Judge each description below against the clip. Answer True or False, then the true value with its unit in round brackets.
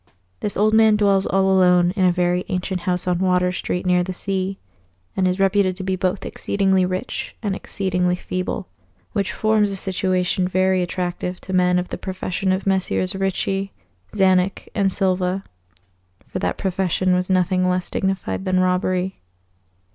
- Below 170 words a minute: True (160 wpm)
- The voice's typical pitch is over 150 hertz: True (185 Hz)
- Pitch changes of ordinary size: False (1.1 semitones)